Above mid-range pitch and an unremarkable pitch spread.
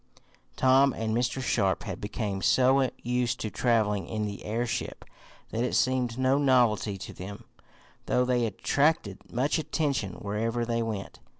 No: low, 120 Hz; average, 3.5 semitones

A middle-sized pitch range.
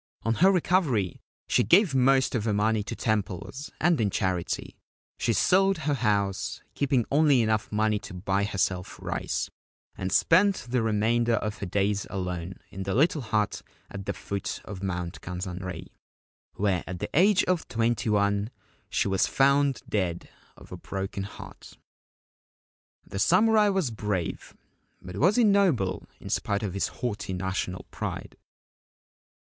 No: wide, 6.3 semitones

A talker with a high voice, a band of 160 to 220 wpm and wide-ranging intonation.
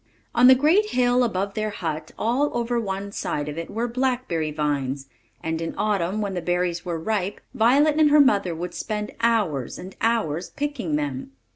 Yes: high, 200 Hz; average, 180 wpm; wide, 6.7 semitones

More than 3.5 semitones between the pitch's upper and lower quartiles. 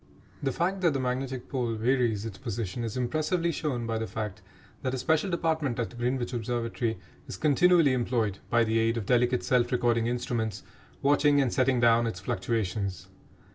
No: average, 3.0 semitones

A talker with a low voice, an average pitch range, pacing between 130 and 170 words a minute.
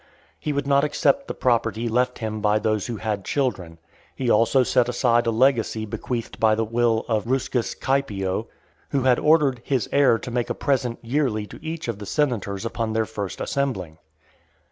No: low, 115 Hz; average, 3.5 semitones; average, 185 wpm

